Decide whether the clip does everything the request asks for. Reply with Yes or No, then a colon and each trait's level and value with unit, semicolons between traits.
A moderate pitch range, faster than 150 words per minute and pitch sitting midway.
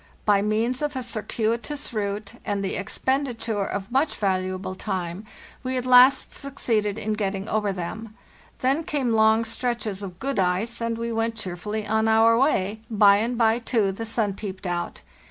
No: average, 3.0 semitones; average, 170 wpm; high, 220 Hz